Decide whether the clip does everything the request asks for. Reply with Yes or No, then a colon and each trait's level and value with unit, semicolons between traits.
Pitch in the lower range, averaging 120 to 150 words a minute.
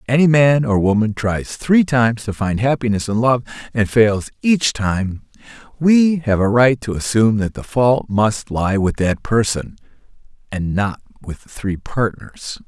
No: low, 115 Hz; average, 175 wpm